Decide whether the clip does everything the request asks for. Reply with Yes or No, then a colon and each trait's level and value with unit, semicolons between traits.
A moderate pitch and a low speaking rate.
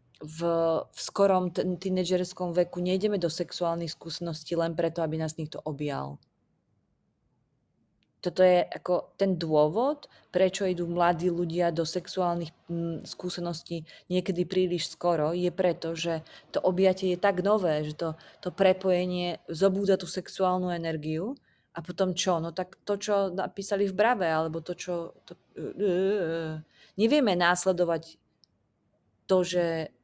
No: medium, 180 Hz; average, 140 wpm